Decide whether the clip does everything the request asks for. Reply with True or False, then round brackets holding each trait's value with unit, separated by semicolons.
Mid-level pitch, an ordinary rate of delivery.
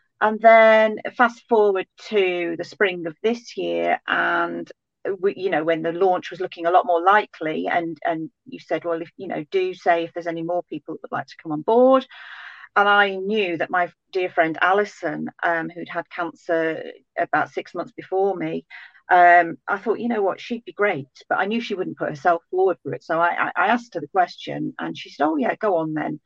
False (180 Hz; 220 wpm)